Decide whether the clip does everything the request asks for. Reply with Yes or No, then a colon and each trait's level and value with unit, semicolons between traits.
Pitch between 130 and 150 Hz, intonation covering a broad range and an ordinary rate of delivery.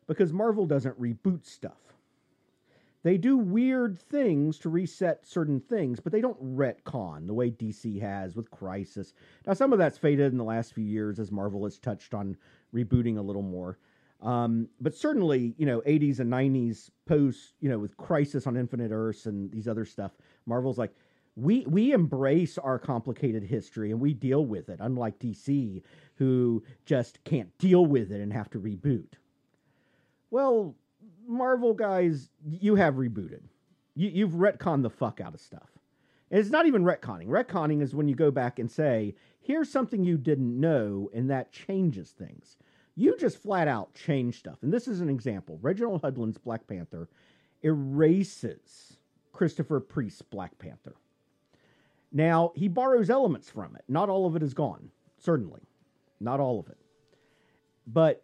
Yes: medium, 140 Hz; wide, 7.3 semitones; average, 165 wpm